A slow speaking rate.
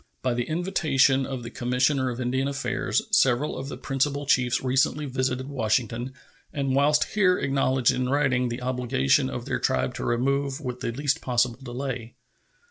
No: average, 165 wpm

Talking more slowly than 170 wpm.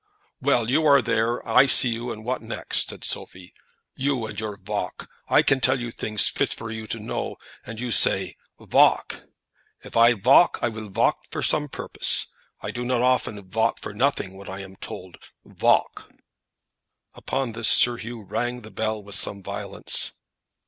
No: average, 175 wpm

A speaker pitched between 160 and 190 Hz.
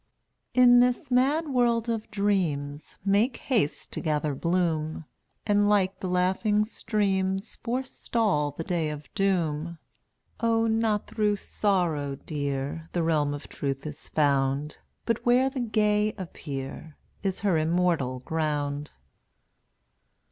Yes: medium, 185 Hz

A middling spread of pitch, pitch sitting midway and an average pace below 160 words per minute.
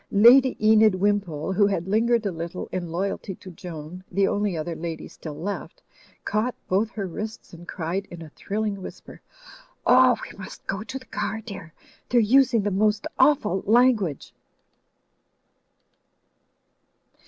No: average, 3.8 semitones; high, 200 Hz; average, 150 wpm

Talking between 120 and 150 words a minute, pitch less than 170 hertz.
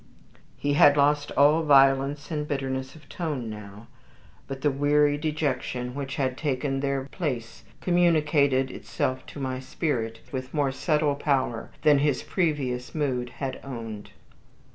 Yes: average, 140 wpm; medium, 140 Hz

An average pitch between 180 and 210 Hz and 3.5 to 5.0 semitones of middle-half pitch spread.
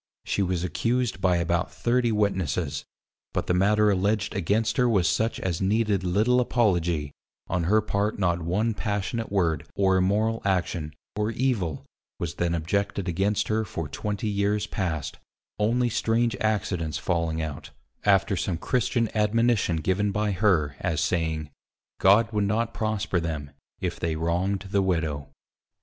No: low, 100 Hz; average, 4.0 semitones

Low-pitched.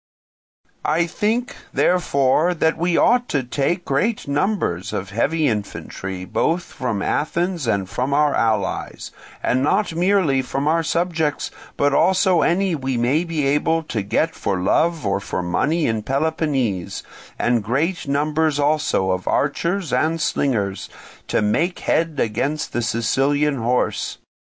No: medium, 145 Hz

